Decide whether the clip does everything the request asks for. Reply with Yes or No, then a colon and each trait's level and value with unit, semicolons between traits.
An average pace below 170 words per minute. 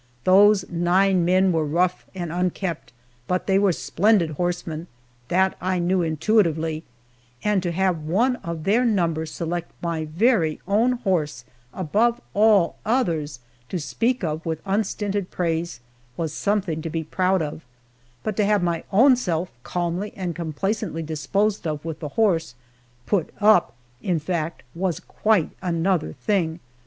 Yes: average, 145 wpm